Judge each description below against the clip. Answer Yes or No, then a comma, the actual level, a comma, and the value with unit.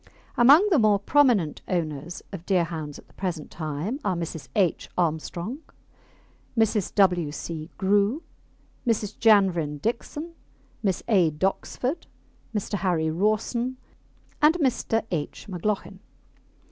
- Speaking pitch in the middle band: No, high, 195 Hz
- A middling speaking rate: No, slow, 115 wpm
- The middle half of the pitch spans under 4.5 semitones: No, average, 5.2 semitones